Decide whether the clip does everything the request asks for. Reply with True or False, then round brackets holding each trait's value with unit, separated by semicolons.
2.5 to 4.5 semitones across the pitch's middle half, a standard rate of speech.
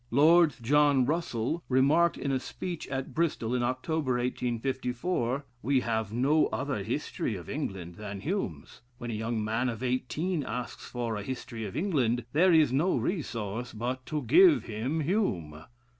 False (5.1 semitones; 160 wpm)